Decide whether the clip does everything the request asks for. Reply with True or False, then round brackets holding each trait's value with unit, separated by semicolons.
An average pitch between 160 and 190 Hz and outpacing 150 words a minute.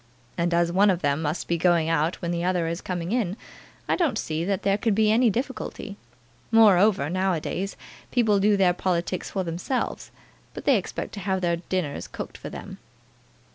True (185 Hz; 195 wpm)